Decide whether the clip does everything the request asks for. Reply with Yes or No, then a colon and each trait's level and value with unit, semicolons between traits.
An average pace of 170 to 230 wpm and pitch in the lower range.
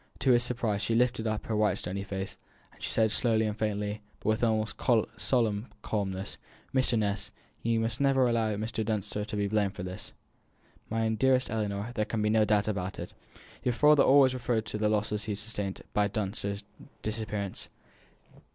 Yes: average, 185 wpm; low, 110 Hz